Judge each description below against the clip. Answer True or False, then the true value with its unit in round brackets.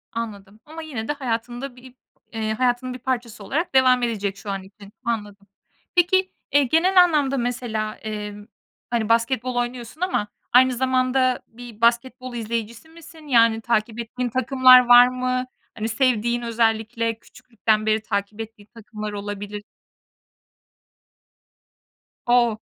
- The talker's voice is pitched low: False (235 Hz)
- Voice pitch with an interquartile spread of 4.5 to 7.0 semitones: False (2.8 semitones)